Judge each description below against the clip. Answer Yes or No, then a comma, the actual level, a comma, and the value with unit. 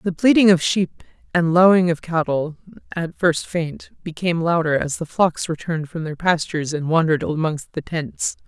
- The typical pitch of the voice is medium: Yes, medium, 165 Hz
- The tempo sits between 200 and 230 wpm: No, average, 175 wpm